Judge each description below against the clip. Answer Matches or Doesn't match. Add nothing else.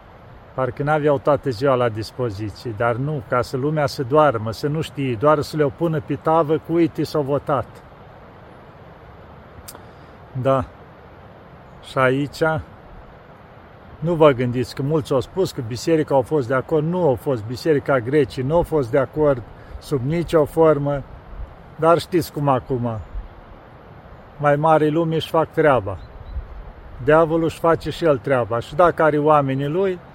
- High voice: Doesn't match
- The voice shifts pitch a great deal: Doesn't match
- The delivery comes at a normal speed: Matches